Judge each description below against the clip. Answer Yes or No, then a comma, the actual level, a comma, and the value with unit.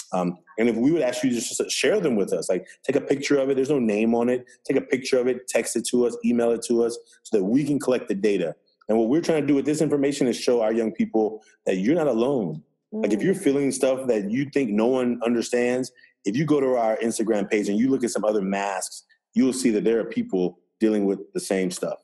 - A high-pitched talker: No, low, 120 Hz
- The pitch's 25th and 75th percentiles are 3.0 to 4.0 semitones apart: No, average, 4.5 semitones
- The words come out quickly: Yes, fast, 265 wpm